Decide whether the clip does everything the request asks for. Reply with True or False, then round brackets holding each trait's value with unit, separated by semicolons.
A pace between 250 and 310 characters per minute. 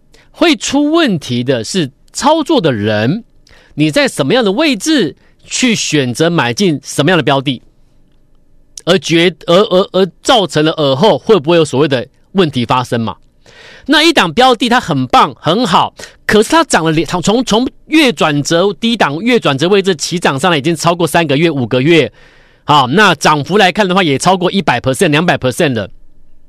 True (280 characters per minute)